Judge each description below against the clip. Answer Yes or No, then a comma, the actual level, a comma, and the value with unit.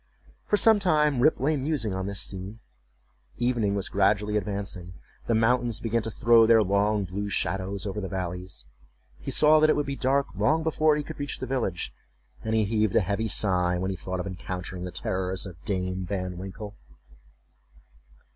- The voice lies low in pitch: Yes, low, 105 Hz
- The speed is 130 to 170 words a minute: No, average, 185 wpm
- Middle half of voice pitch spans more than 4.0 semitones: Yes, average, 4.7 semitones